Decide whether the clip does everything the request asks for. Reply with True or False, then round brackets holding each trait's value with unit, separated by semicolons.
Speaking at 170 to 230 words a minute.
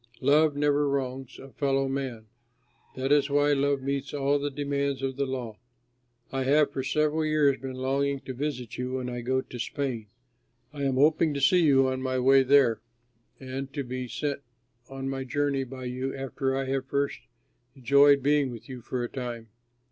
True (185 wpm)